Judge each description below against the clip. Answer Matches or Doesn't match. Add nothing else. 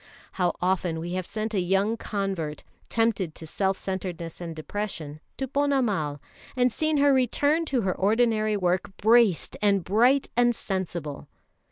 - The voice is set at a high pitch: Matches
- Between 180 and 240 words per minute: Doesn't match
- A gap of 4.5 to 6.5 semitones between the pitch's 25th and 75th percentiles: Matches